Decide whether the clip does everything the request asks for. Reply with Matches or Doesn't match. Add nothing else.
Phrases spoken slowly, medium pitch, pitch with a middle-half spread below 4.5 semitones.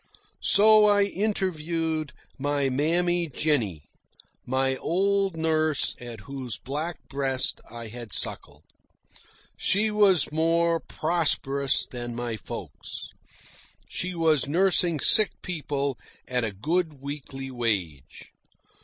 Doesn't match